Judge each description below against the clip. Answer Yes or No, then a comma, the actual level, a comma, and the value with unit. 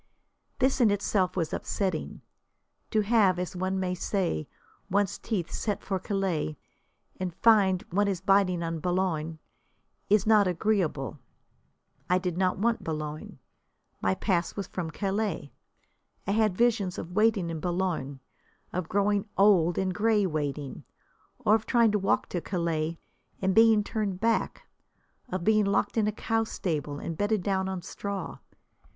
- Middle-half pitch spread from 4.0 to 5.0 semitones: No, average, 3.4 semitones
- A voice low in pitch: No, high, 190 Hz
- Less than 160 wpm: Yes, average, 150 wpm